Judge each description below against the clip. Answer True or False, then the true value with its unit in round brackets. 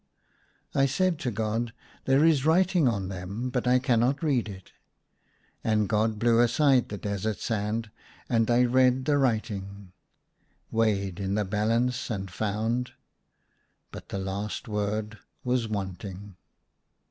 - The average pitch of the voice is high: False (110 Hz)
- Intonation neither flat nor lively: True (3.6 semitones)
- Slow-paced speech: False (145 wpm)